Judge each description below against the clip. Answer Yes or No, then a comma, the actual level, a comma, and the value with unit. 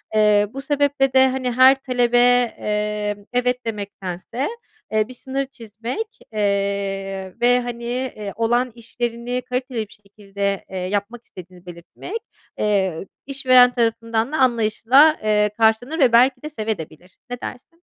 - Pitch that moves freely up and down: No, average, 3.6 semitones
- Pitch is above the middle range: Yes, high, 230 Hz